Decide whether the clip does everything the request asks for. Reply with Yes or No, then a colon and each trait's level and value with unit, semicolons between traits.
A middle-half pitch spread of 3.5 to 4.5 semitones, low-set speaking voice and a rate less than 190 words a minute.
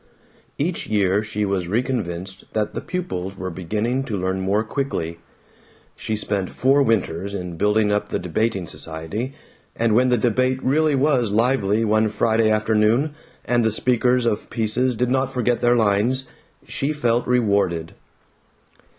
Yes: average, 4.0 semitones; low, 110 Hz; average, 150 wpm